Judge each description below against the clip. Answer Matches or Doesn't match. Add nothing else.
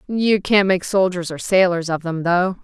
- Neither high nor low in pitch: Matches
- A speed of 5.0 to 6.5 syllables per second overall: Doesn't match